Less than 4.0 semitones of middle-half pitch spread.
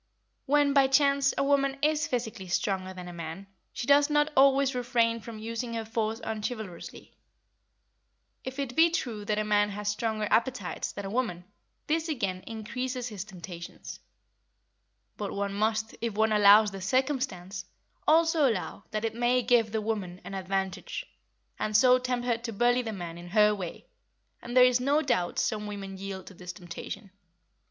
No: average, 4.4 semitones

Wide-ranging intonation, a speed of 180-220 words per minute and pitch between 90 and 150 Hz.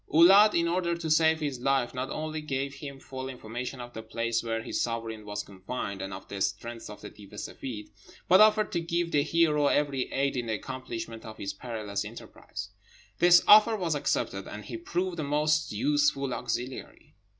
Yes: wide, 5.7 semitones; average, 195 wpm; low, 135 Hz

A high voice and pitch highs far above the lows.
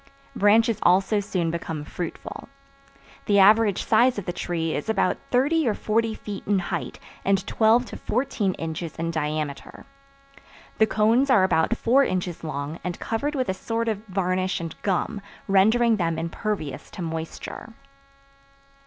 No: high, 195 Hz; average, 4.9 semitones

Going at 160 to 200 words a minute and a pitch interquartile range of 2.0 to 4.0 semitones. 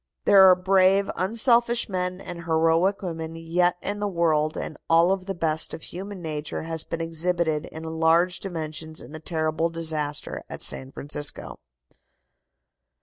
No: average, 150 wpm; narrow, 2.6 semitones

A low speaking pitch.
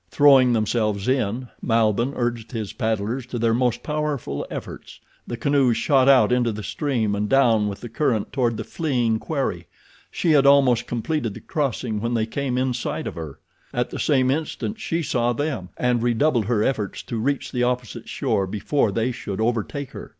Yes: low, 120 Hz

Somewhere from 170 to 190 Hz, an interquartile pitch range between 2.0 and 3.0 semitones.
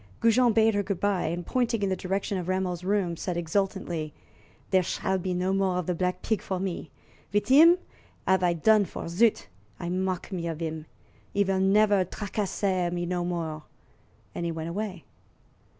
Yes: medium, 185 Hz; average, 2.7 semitones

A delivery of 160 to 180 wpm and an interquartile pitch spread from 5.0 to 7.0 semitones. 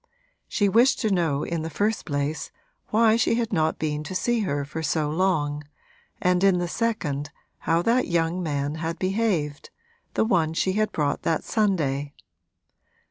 Yes: average, 165 wpm; wide, 5.5 semitones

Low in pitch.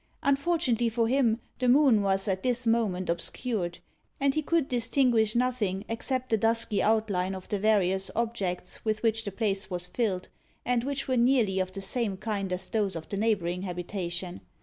No: high, 220 Hz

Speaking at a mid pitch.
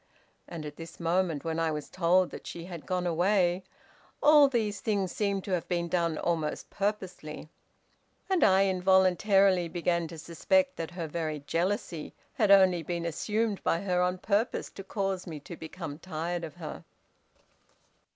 Yes: medium, 180 Hz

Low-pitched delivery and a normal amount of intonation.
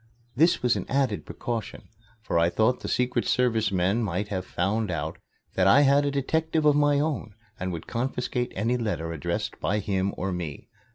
No: low, 110 Hz; wide, 6.0 semitones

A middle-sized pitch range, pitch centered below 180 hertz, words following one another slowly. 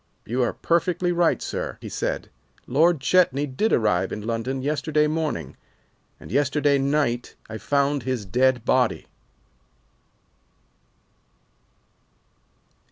Yes: average, 4.1 semitones; low, 135 Hz; slow, 105 wpm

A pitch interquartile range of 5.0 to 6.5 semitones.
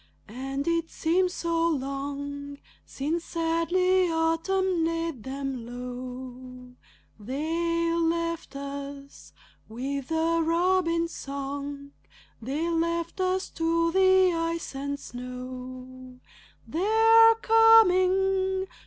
No: average, 3.8 semitones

